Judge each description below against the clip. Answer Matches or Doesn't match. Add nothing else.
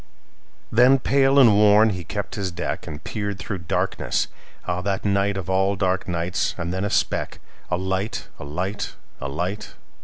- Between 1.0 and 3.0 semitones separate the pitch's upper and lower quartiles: Matches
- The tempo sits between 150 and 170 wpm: Matches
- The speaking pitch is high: Doesn't match